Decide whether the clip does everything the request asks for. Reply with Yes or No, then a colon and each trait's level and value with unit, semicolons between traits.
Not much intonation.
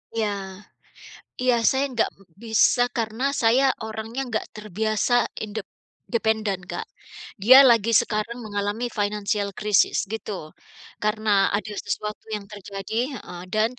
Yes: narrow, 1.8 semitones